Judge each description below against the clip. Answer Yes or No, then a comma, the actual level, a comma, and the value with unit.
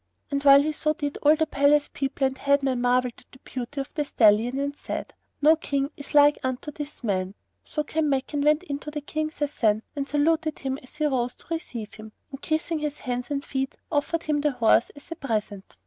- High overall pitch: Yes, very high, 280 Hz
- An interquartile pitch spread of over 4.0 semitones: No, average, 2.8 semitones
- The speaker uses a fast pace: Yes, fast, 215 wpm